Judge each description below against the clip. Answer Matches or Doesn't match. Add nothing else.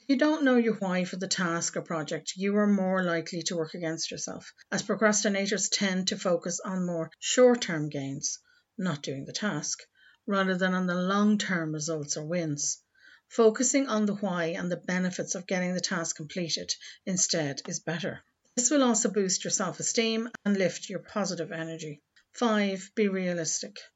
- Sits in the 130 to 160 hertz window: Doesn't match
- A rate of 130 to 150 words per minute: Doesn't match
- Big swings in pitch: Doesn't match